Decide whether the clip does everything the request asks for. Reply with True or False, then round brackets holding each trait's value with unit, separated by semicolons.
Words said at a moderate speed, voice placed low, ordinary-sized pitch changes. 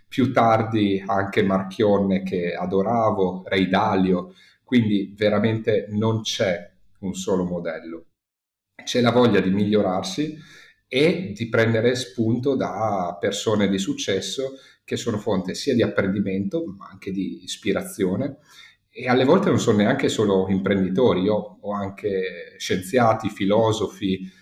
True (125 wpm; 100 Hz; 3.0 semitones)